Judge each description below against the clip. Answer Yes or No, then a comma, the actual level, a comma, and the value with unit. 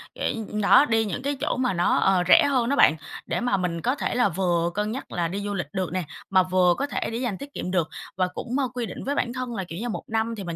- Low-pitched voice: No, high, 205 Hz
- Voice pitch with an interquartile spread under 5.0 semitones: No, average, 5.3 semitones